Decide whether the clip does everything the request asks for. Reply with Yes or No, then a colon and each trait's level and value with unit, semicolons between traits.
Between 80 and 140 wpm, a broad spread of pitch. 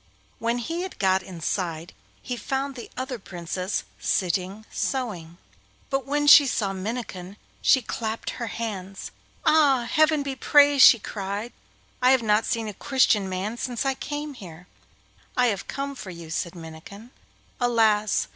No: average, 150 wpm; wide, 5.7 semitones